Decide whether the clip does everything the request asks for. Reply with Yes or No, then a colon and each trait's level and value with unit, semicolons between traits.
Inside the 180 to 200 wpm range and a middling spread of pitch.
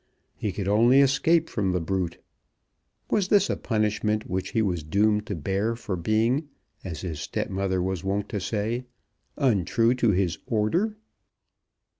No: average, 150 wpm; average, 3.9 semitones